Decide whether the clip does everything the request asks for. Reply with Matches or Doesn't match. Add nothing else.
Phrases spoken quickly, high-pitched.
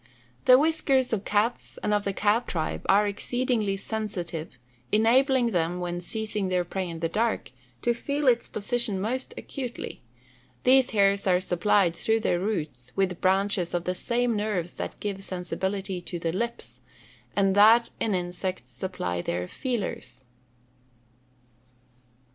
Doesn't match